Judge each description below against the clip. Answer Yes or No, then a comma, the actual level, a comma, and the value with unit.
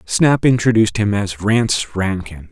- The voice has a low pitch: Yes, low, 105 Hz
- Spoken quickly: No, average, 145 wpm